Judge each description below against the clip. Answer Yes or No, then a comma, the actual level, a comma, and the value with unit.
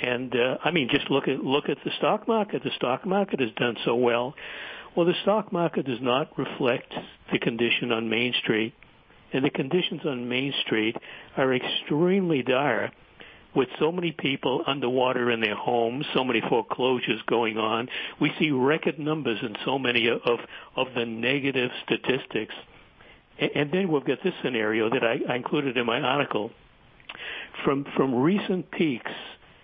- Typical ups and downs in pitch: No, wide, 5.7 semitones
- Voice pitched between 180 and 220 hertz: No, low, 135 Hz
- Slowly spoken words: No, average, 170 wpm